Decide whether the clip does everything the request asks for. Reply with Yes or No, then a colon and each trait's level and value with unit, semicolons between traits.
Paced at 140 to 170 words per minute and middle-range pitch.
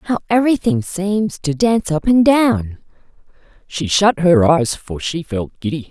Yes: average, 165 wpm; medium, 170 Hz